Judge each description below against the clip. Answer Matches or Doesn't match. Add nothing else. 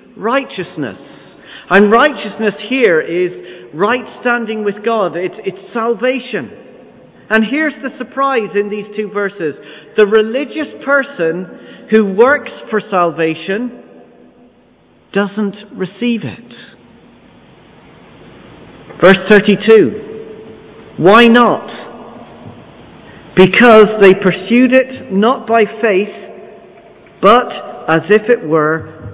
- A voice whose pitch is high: Matches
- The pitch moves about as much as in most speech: Matches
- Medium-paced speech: Doesn't match